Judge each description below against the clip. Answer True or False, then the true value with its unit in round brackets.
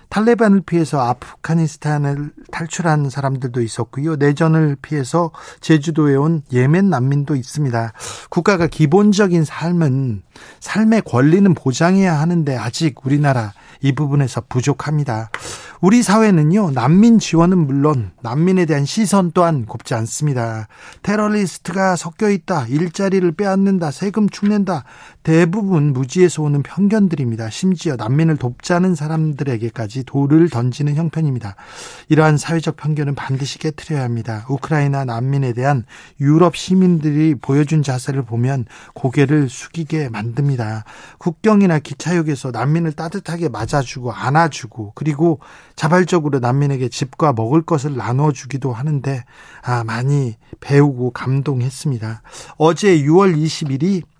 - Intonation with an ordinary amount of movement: True (4.3 semitones)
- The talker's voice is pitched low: False (150 Hz)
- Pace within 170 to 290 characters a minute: False (325 characters per minute)